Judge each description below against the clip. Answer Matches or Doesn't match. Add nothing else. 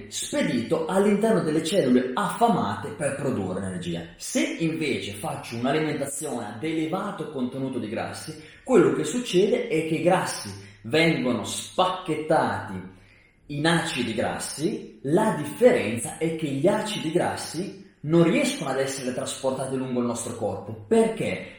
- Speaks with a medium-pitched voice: Matches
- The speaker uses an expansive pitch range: Matches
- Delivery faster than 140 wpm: Doesn't match